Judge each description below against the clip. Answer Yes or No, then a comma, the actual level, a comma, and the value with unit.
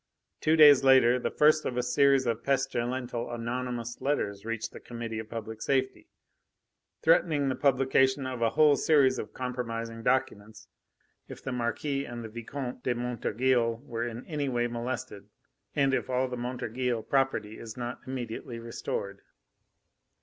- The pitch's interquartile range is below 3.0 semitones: Yes, narrow, 2.4 semitones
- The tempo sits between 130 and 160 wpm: Yes, average, 150 wpm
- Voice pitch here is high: No, low, 125 Hz